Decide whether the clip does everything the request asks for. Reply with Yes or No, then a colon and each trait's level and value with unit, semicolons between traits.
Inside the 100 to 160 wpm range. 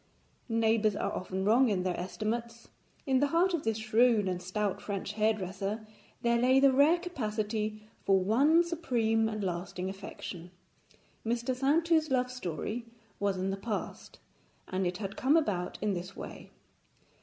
Yes: average, 155 wpm